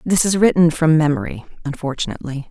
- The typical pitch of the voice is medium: Yes, medium, 155 Hz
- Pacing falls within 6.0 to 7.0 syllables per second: Yes, 6.3 syllables/s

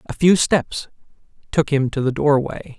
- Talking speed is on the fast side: No, average, 170 wpm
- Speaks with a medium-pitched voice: Yes, medium, 145 Hz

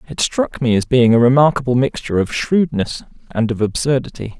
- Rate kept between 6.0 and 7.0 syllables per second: No, 5.6 syllables/s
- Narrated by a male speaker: Yes, male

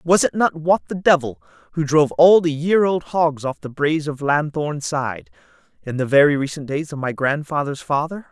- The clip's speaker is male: Yes, male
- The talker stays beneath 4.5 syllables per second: No, 4.9 syllables/s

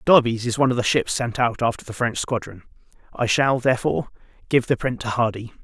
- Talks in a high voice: No, low, 120 Hz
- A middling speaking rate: No, fast, 215 wpm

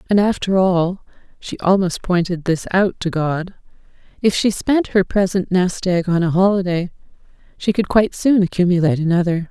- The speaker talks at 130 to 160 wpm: Yes, average, 150 wpm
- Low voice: No, medium, 185 Hz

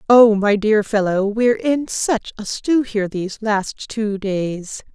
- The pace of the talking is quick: No, average, 170 wpm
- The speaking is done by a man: No, female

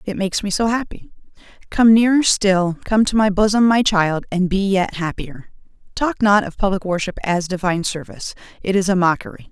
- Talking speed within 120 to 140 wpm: No, average, 175 wpm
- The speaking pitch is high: Yes, high, 195 Hz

